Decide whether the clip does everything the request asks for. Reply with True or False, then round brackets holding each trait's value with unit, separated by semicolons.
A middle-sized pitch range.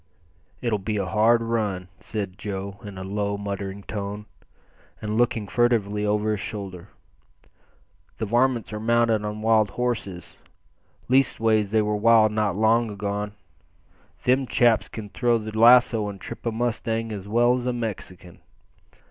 False (2.3 semitones)